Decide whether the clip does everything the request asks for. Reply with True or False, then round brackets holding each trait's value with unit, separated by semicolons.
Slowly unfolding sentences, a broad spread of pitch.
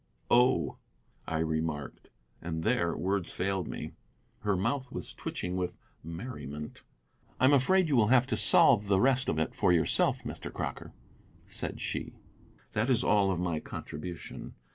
False (155 wpm; 6.9 semitones)